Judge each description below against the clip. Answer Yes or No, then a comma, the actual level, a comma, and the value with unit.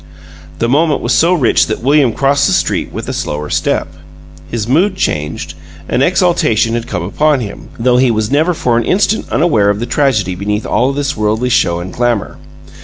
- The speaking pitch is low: Yes, low, 120 Hz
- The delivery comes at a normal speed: Yes, average, 190 wpm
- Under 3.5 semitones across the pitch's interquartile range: No, wide, 5.4 semitones